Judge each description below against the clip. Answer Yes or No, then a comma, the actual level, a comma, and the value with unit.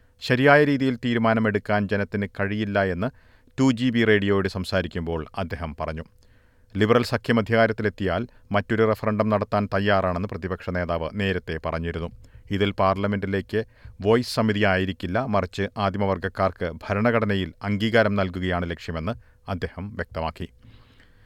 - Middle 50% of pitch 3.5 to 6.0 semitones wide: No, average, 2.8 semitones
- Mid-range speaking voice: No, low, 100 Hz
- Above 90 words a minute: Yes, average, 105 wpm